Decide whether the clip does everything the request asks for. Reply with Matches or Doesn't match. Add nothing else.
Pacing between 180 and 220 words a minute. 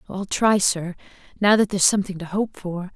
Matches